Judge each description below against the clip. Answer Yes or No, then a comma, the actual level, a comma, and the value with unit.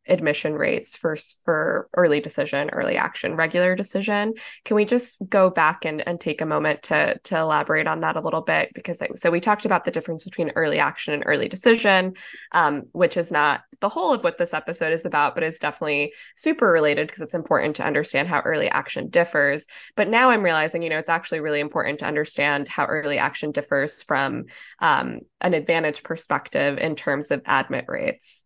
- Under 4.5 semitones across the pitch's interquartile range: No, average, 5.0 semitones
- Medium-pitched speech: Yes, medium, 170 Hz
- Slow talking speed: No, average, 200 wpm